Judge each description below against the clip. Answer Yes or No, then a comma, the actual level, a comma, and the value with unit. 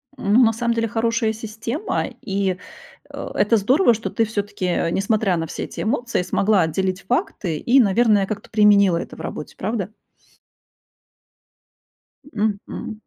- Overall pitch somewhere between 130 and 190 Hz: No, high, 210 Hz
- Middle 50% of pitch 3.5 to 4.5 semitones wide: No, average, 2.8 semitones